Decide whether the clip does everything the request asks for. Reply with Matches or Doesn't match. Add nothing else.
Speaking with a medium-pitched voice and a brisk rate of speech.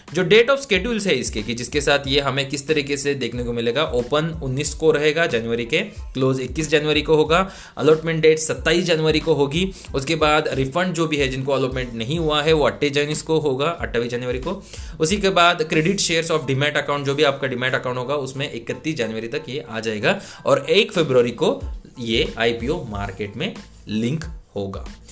Matches